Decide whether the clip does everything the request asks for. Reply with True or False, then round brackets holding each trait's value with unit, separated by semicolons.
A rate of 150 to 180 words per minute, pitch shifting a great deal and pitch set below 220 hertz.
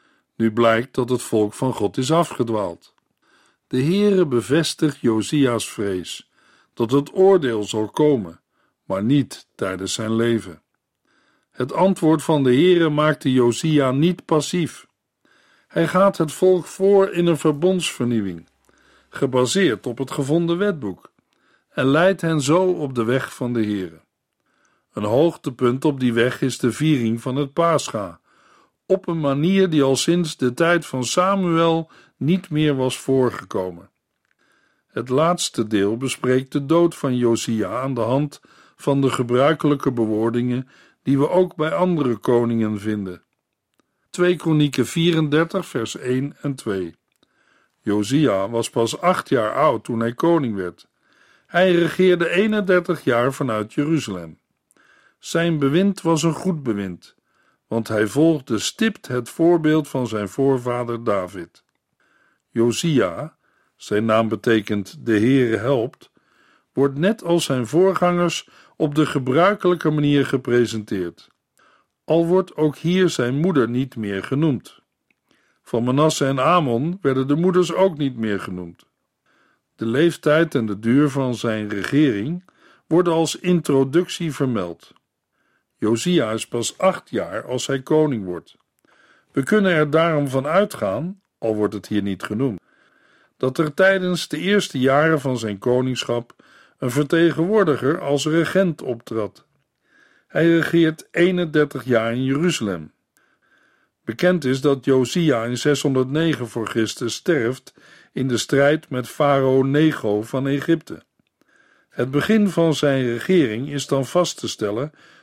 False (135 wpm; 5.9 semitones; 140 Hz)